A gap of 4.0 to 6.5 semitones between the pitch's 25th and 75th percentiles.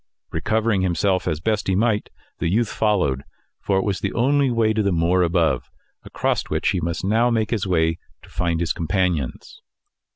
Yes: average, 4.4 semitones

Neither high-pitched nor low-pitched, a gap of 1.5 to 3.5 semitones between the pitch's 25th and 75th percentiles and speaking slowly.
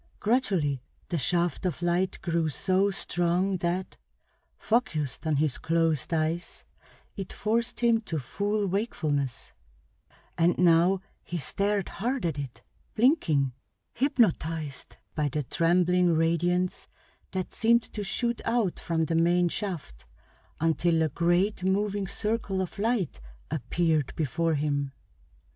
No: medium, 175 Hz; average, 3.9 semitones; slow, 120 wpm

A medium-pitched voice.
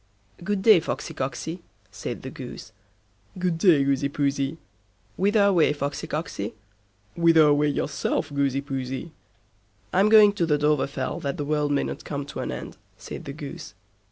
Yes: medium, 150 Hz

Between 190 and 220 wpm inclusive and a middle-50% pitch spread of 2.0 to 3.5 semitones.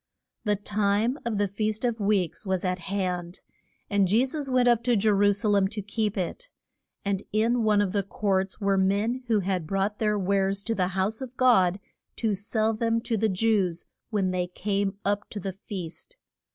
Yes: average, 195 wpm; narrow, 2.4 semitones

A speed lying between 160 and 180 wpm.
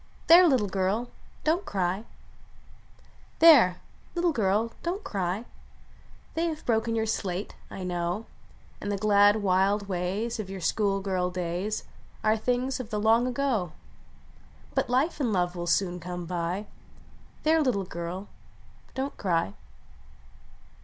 No: average, 140 wpm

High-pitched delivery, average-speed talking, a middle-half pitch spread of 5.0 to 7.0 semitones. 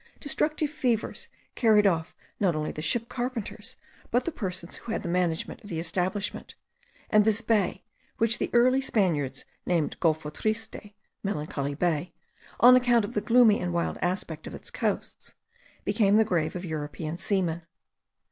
Yes: high, 195 Hz; average, 155 wpm; wide, 5.5 semitones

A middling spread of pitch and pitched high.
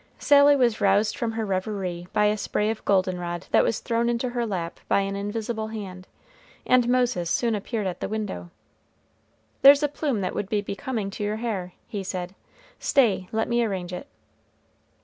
Yes: average, 3.8 semitones; high, 210 Hz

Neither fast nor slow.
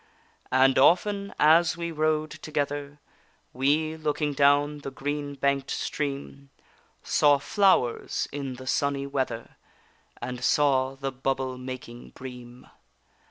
No: slow, 115 wpm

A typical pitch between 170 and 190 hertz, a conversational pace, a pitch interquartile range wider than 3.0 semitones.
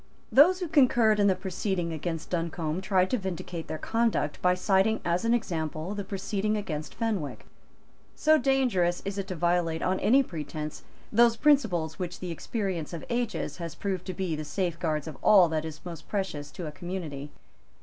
Yes: medium, 185 Hz; average, 180 wpm; average, 4.6 semitones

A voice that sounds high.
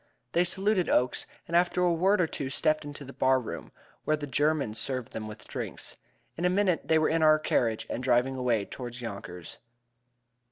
No: medium, 145 Hz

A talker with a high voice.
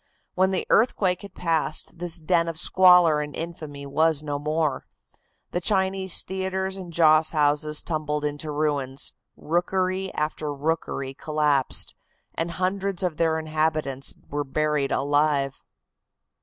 No: medium, 155 Hz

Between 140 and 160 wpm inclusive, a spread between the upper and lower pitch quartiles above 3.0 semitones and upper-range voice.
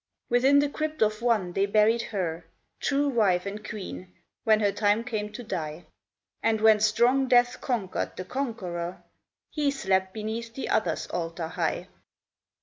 Yes: average, 150 wpm; average, 4.4 semitones; high, 215 Hz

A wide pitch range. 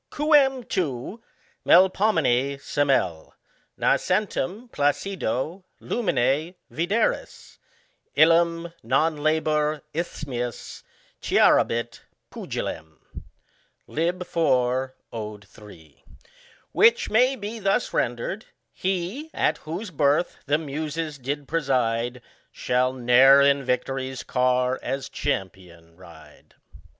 Yes: wide, 6.0 semitones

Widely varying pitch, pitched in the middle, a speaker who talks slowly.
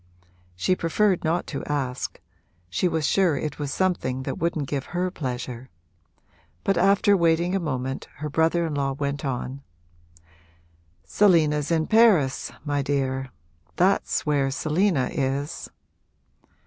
No: average, 4.3 semitones; medium, 150 Hz; slow, 130 wpm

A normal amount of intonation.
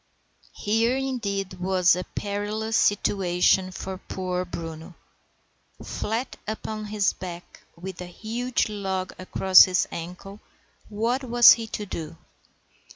Yes: average, 3.2 semitones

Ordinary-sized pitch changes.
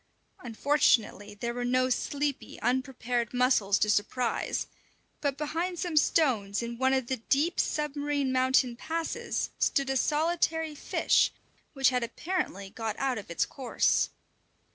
Yes: average, 3.9 semitones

